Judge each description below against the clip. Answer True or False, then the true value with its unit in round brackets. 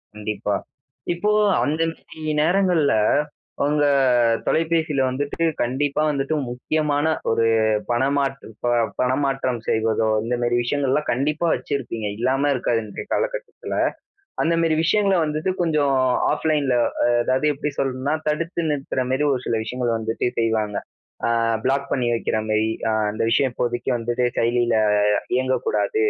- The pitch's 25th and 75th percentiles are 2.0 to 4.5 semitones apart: True (4.2 semitones)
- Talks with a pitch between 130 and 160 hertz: True (135 Hz)